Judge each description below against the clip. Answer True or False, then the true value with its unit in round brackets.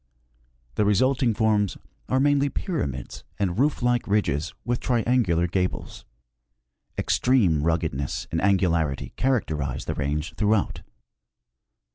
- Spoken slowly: True (105 wpm)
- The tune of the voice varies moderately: False (7.2 semitones)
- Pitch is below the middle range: True (100 Hz)